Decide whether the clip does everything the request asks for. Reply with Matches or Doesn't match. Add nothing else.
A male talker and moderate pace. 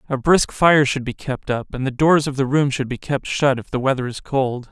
Doesn't match